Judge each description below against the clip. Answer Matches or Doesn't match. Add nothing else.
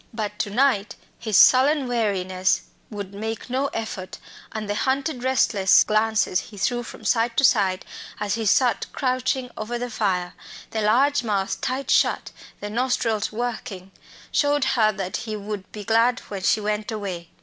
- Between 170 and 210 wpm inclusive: Doesn't match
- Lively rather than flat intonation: Doesn't match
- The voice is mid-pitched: Doesn't match